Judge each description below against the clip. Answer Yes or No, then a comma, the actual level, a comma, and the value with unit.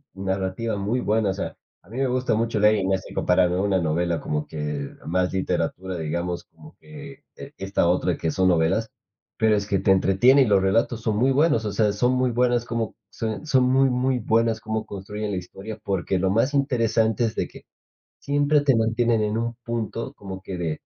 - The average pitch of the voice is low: Yes, low, 110 Hz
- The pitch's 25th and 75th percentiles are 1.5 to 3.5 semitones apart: No, average, 4.3 semitones